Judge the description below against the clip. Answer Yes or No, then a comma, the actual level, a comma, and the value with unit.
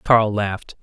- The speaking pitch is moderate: No, low, 105 Hz